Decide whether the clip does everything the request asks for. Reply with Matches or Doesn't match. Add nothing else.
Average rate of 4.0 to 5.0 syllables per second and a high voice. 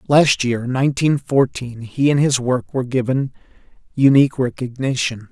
Doesn't match